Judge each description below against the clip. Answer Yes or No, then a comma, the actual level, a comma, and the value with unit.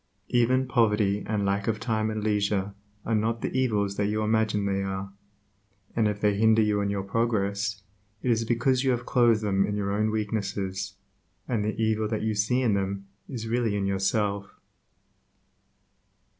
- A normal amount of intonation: No, narrow, 2.1 semitones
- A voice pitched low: Yes, low, 105 Hz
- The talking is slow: No, average, 175 wpm